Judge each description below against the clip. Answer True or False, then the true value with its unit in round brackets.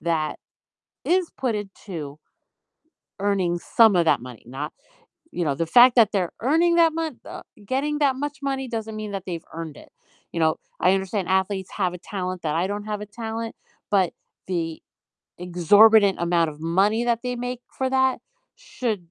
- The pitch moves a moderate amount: False (6.0 semitones)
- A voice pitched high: True (200 Hz)